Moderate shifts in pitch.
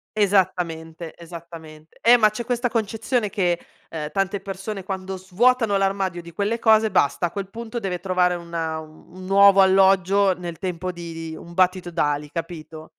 Yes: average, 3.0 semitones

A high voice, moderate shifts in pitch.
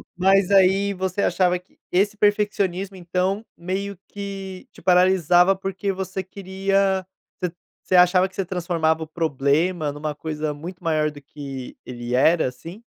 No: medium, 180 Hz; average, 3.3 semitones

